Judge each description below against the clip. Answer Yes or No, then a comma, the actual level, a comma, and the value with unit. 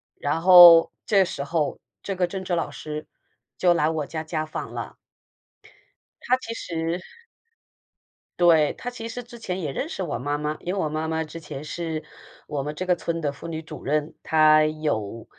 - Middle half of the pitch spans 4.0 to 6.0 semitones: No, average, 2.8 semitones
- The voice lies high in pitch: No, medium, 160 Hz